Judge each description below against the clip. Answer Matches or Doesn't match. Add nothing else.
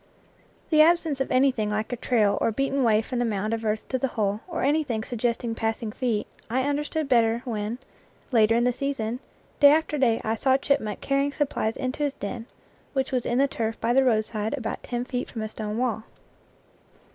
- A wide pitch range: Doesn't match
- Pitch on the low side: Doesn't match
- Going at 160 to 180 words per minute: Doesn't match